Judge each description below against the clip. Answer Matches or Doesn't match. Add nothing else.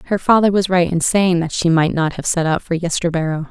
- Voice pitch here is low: Doesn't match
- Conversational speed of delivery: Doesn't match